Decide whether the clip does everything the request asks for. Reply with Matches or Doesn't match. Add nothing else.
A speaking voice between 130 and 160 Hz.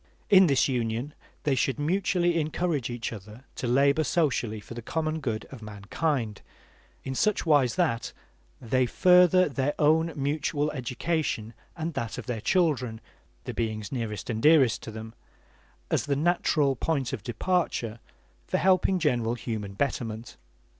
Matches